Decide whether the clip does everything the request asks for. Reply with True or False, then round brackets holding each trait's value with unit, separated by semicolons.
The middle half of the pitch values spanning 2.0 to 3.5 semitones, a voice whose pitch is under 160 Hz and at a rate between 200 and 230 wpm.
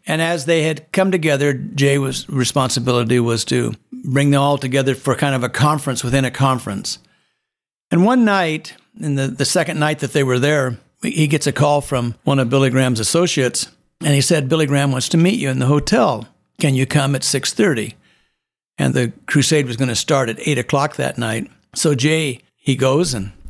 True (2.9 semitones; 140 Hz; 205 wpm)